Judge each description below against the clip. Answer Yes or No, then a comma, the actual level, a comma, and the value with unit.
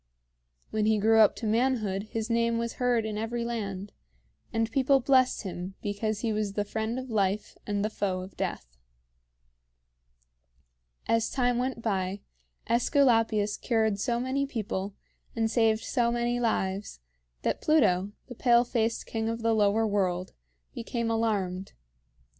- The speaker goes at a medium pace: Yes, average, 145 wpm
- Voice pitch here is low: No, high, 225 Hz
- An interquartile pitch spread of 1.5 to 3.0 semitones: Yes, average, 2.7 semitones